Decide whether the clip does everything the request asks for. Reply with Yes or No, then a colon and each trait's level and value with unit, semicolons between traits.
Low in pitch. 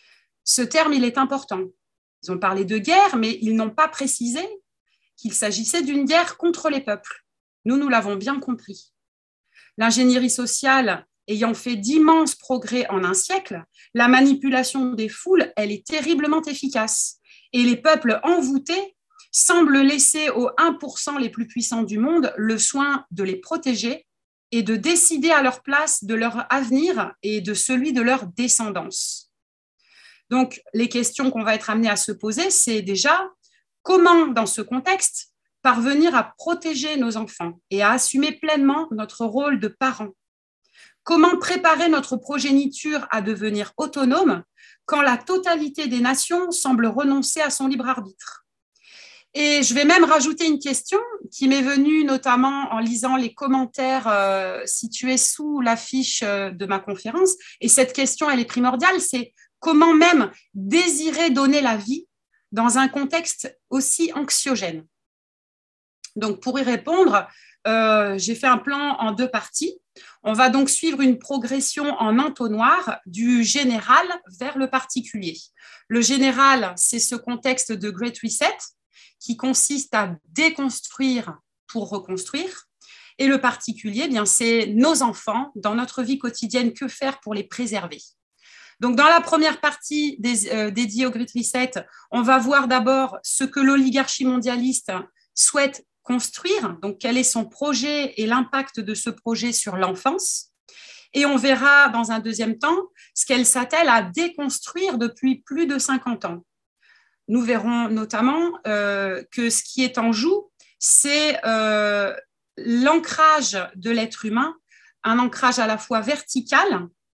No: very high, 255 Hz